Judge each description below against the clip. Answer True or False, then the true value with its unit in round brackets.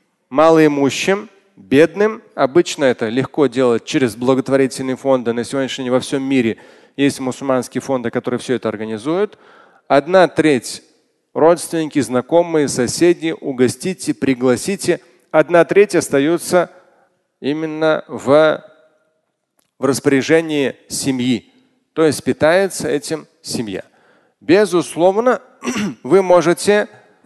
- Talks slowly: True (100 wpm)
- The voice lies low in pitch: False (150 Hz)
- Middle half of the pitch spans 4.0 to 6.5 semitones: True (4.8 semitones)